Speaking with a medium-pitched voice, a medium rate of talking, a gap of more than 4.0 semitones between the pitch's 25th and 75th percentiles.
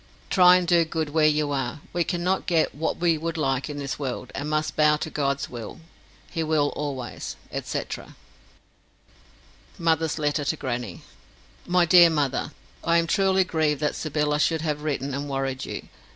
No: medium, 150 Hz; average, 170 wpm; average, 2.7 semitones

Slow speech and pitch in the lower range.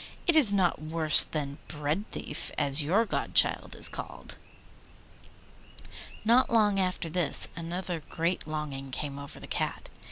No: slow, 130 wpm; medium, 165 Hz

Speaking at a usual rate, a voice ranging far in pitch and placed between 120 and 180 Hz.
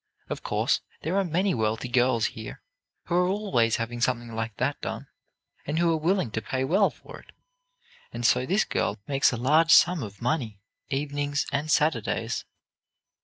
Yes: average, 170 wpm; wide, 6.0 semitones; low, 135 Hz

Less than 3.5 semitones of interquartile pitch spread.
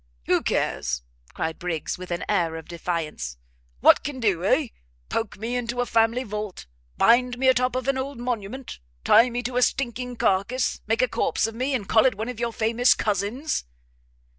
No: average, 4.3 semitones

